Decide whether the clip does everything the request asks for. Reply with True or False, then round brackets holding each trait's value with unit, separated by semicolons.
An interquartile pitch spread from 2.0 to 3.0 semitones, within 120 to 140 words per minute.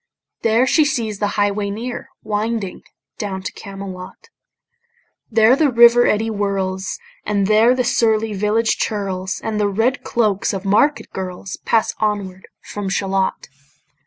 True (2.6 semitones; 135 wpm)